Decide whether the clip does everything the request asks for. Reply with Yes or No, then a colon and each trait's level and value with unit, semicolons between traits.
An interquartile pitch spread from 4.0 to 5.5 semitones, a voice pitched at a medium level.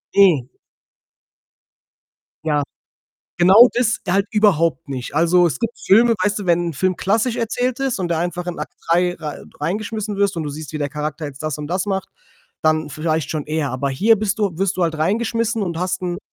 Yes: average, 4.7 semitones; medium, 175 Hz